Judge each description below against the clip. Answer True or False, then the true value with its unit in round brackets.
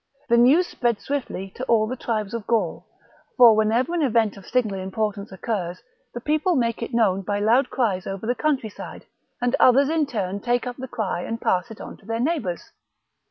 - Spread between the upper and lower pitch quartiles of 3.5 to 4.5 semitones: True (3.8 semitones)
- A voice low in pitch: False (230 Hz)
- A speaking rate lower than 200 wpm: False (205 wpm)